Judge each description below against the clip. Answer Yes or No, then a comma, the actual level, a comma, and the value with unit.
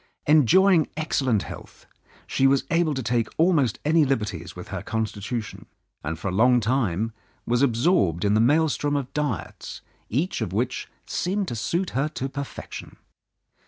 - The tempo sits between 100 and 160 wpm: Yes, average, 155 wpm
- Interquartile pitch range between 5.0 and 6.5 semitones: Yes, wide, 5.5 semitones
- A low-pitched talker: Yes, low, 130 Hz